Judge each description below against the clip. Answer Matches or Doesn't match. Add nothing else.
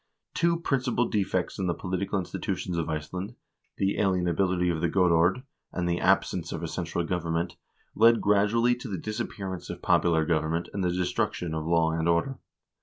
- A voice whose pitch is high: Doesn't match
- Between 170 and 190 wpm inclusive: Matches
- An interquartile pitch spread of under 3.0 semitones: Doesn't match